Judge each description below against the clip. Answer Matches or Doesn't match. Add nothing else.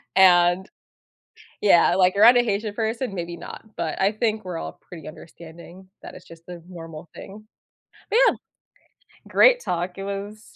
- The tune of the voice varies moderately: Matches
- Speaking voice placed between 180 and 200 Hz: Matches